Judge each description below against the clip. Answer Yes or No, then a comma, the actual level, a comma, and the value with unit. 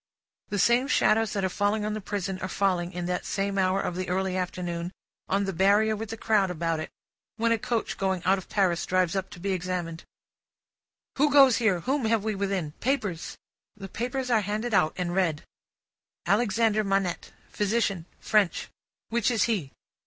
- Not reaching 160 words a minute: No, average, 180 wpm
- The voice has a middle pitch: No, high, 195 Hz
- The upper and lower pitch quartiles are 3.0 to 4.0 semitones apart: Yes, average, 3.3 semitones